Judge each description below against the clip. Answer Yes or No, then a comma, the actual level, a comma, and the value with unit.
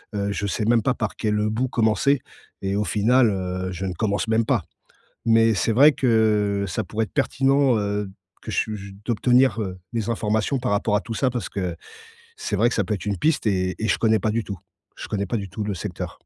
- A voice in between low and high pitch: No, low, 110 Hz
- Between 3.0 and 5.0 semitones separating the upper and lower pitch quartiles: No, narrow, 2.6 semitones